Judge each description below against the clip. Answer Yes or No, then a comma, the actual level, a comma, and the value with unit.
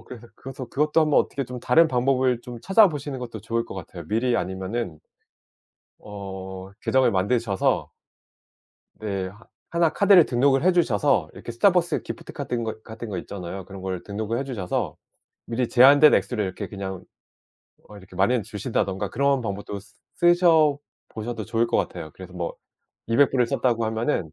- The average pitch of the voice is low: Yes, low, 115 Hz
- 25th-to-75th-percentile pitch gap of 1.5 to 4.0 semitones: No, wide, 5.5 semitones